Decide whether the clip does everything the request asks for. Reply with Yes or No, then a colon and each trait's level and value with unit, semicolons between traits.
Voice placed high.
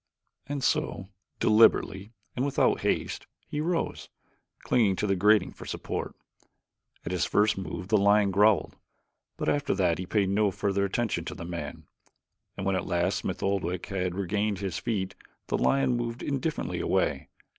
No: low, 100 Hz